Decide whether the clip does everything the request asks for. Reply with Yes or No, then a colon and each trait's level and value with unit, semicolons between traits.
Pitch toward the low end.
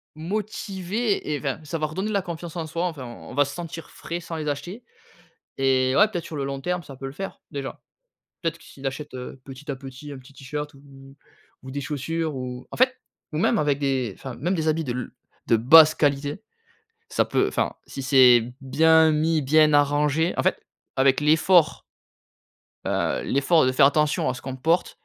No: medium, 150 Hz